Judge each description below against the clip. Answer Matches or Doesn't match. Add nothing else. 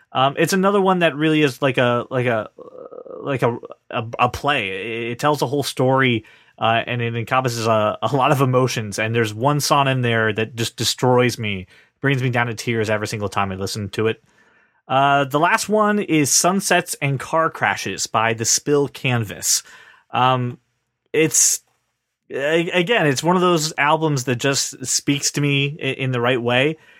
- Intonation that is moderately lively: Matches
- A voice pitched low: Matches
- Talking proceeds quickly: Doesn't match